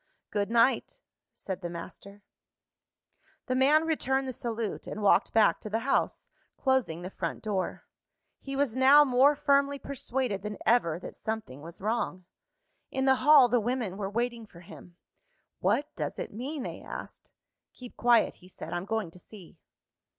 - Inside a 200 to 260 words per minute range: No, average, 165 wpm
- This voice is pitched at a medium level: No, high, 230 Hz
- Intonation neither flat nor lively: Yes, average, 5.0 semitones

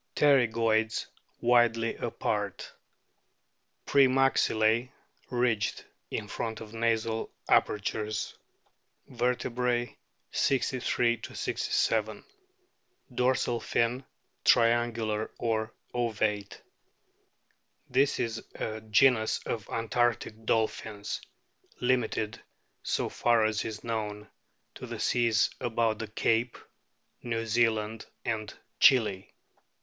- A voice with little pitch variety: Yes, narrow, 1.7 semitones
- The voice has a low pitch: Yes, low, 115 Hz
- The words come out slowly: Yes, slow, 85 wpm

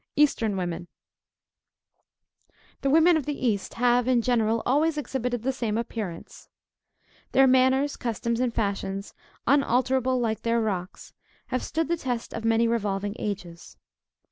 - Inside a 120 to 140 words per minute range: Yes, slow, 135 wpm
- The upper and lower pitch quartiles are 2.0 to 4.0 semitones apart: Yes, average, 3.5 semitones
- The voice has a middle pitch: No, high, 235 Hz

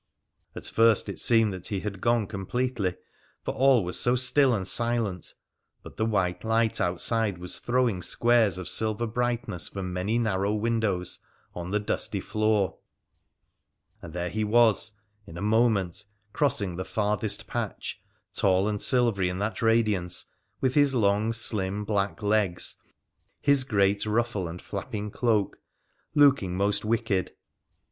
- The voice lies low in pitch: Yes, low, 105 Hz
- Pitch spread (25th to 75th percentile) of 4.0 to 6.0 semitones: No, average, 3.5 semitones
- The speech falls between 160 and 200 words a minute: No, average, 150 wpm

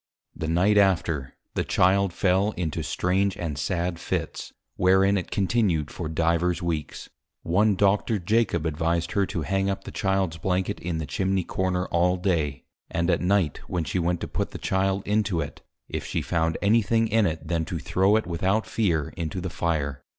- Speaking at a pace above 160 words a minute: Yes, average, 185 wpm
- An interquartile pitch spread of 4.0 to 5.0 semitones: No, average, 2.9 semitones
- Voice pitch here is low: Yes, very low, 90 Hz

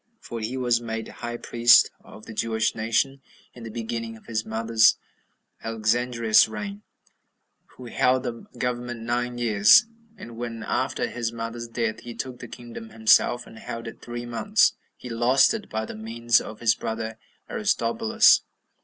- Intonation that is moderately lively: No, narrow, 1.4 semitones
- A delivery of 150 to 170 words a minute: Yes, average, 160 wpm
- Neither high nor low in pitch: No, low, 115 Hz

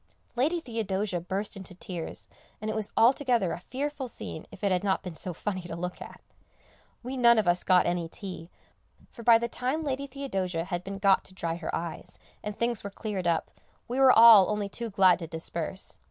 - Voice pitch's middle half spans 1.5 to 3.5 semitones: No, average, 4.8 semitones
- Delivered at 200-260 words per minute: Yes, fast, 205 wpm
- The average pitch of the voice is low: No, high, 200 Hz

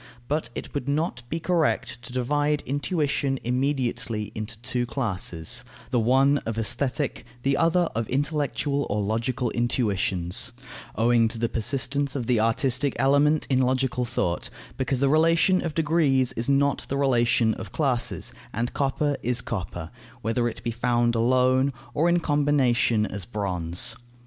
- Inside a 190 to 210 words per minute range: No, average, 150 wpm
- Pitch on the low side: Yes, low, 125 Hz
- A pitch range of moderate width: Yes, average, 3.7 semitones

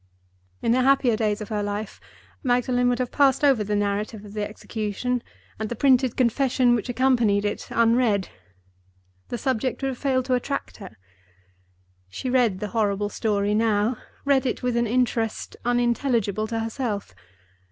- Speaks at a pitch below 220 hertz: No, high, 235 Hz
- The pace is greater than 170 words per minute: No, average, 155 wpm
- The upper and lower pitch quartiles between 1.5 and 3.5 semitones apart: Yes, average, 3.2 semitones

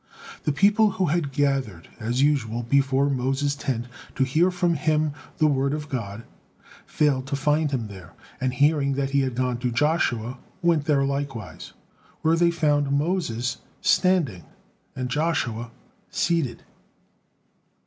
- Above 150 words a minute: No, average, 140 wpm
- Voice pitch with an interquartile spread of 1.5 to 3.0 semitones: No, average, 3.5 semitones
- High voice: No, medium, 140 Hz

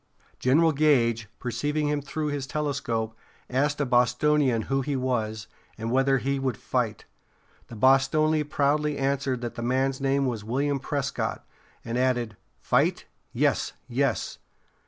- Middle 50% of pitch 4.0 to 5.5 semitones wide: No, average, 3.0 semitones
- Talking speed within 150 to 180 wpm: No, slow, 135 wpm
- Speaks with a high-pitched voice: No, low, 135 Hz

